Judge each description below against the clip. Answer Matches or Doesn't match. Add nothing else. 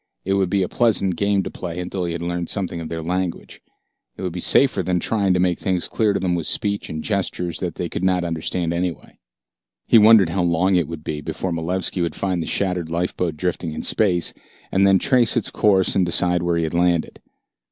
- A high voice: Doesn't match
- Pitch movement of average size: Doesn't match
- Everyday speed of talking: Doesn't match